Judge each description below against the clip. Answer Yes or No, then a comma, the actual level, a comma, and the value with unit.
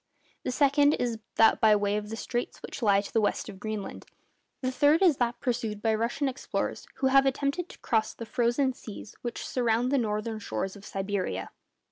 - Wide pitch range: No, average, 3.9 semitones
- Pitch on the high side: Yes, high, 230 Hz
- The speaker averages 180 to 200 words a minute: Yes, average, 195 wpm